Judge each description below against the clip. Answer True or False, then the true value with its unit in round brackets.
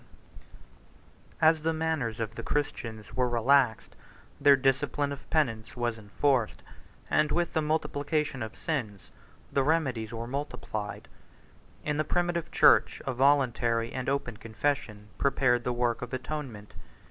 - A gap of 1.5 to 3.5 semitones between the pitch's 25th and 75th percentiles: False (4.2 semitones)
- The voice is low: True (130 Hz)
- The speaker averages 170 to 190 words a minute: False (140 wpm)